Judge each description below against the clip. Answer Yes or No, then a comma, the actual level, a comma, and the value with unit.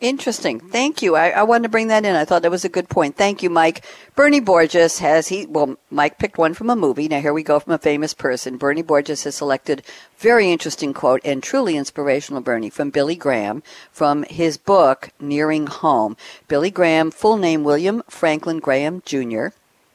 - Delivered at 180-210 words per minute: Yes, average, 200 wpm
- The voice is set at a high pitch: No, medium, 160 Hz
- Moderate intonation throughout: Yes, average, 4.4 semitones